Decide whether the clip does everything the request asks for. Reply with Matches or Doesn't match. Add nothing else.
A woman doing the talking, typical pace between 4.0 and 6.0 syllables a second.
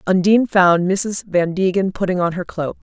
Matches